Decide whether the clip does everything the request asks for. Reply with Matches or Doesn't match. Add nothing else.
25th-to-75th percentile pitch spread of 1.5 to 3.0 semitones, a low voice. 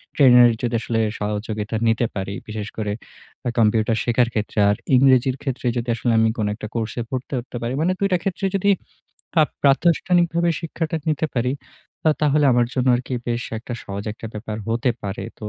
Doesn't match